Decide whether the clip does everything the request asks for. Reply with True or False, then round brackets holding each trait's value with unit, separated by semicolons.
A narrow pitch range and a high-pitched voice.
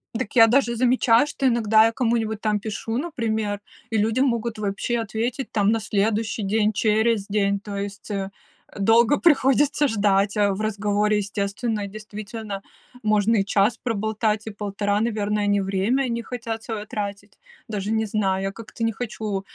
True (2.1 semitones; 215 Hz)